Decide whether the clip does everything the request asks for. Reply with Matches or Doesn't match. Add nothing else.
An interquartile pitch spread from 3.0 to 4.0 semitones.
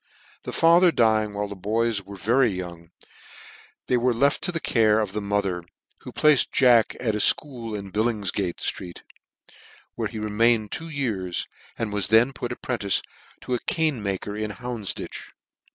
Matches